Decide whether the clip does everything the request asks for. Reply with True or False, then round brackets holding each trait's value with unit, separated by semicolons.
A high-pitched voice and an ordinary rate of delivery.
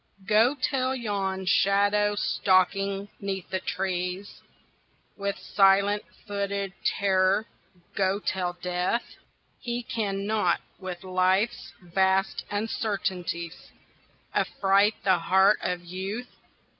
False (195 Hz; 95 wpm)